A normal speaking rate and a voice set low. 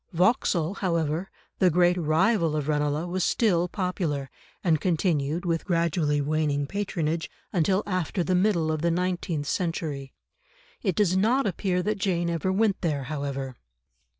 No: average, 145 wpm; medium, 170 Hz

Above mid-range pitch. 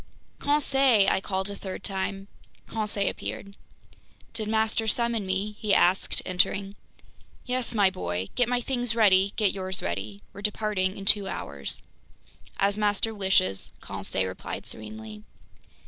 Yes: high, 200 Hz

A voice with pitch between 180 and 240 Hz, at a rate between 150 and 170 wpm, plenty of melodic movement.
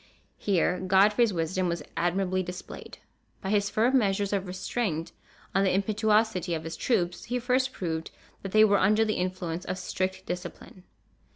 No: high, 190 Hz; average, 160 wpm; average, 2.9 semitones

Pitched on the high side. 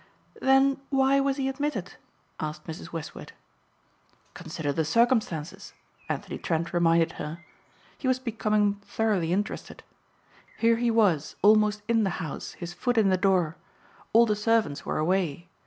Yes: high, 205 Hz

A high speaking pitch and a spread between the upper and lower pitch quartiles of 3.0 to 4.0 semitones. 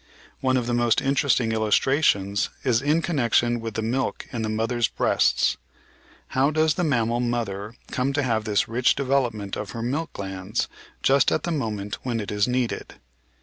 No: low, 120 Hz; average, 3.5 semitones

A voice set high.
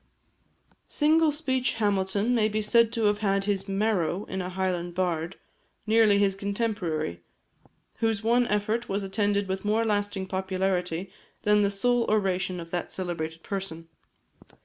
Yes: high, 200 Hz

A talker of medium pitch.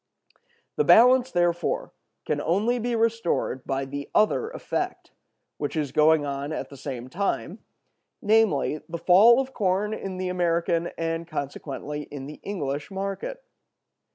Yes: medium, 175 Hz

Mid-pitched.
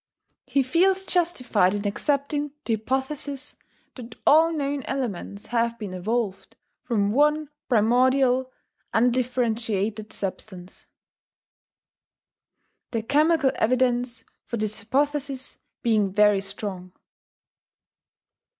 No: high, 245 Hz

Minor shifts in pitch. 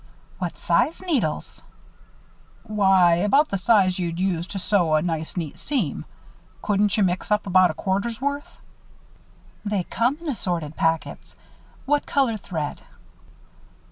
No: average, 4.8 semitones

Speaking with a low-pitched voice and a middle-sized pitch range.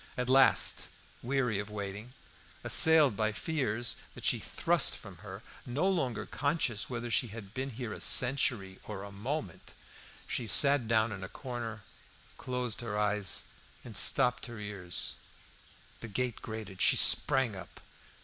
Yes: low, 115 Hz; average, 3.6 semitones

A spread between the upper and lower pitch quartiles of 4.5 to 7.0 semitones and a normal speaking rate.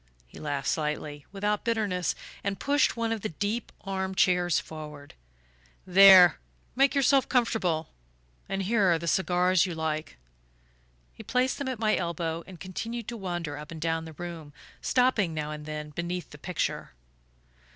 Yes: average, 4.8 semitones; average, 160 wpm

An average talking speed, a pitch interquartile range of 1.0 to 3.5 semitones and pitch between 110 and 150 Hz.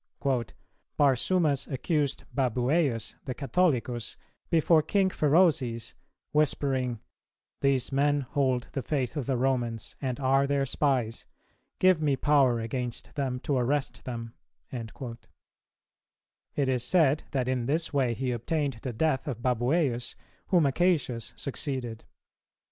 No: slow, 120 wpm; average, 3.1 semitones; low, 135 Hz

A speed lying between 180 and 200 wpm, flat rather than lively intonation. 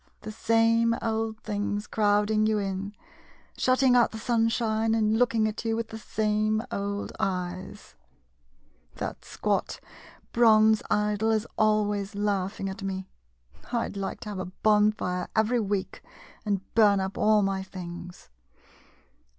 No: average, 140 wpm; narrow, 1.9 semitones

